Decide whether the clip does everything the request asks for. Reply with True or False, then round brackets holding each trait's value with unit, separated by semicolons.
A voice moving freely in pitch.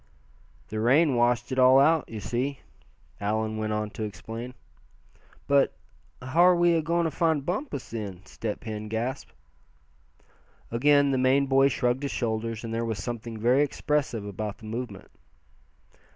False (4.3 semitones)